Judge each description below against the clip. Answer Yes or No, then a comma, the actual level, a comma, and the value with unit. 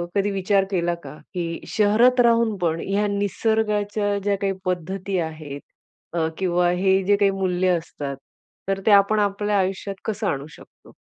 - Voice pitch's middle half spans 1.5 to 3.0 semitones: Yes, average, 2.7 semitones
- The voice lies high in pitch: Yes, high, 195 Hz